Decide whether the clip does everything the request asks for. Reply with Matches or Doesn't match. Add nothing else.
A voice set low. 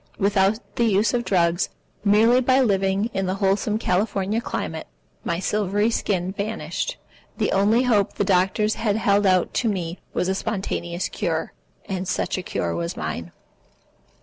Doesn't match